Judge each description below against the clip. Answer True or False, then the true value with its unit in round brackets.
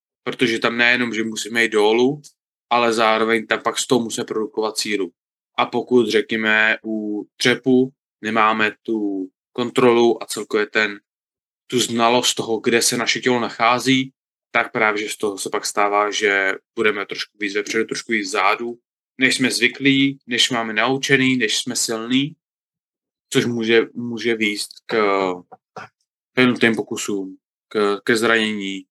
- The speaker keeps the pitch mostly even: True (2.3 semitones)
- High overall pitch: False (115 Hz)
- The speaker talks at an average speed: True (145 wpm)